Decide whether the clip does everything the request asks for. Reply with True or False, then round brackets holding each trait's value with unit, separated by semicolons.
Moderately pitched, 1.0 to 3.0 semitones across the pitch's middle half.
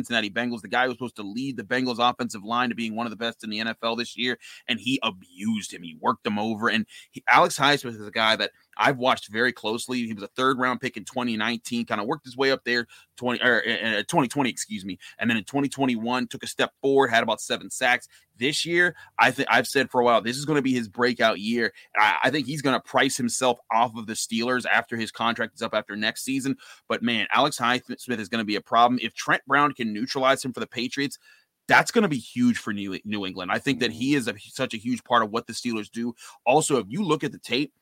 False (120 Hz; 2.7 semitones)